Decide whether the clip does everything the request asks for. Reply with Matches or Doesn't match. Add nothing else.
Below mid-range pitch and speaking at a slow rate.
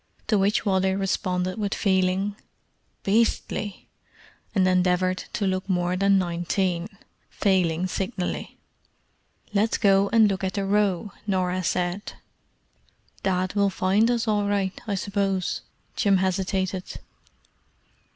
Doesn't match